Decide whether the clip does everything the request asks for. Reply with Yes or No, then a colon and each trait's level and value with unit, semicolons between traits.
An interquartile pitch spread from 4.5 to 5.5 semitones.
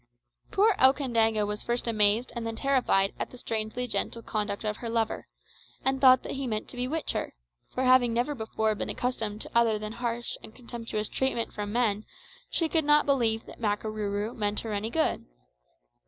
No: average, 2.9 semitones